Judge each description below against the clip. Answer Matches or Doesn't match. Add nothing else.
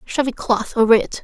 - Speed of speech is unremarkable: Doesn't match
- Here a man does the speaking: Doesn't match